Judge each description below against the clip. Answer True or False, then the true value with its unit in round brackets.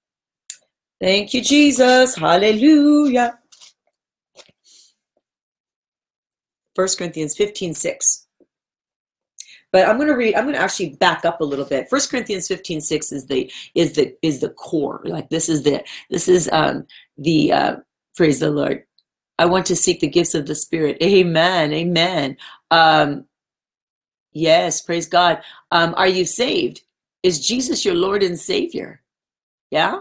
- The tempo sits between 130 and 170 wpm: True (140 wpm)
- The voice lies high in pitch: False (180 Hz)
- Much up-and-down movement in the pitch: True (6.6 semitones)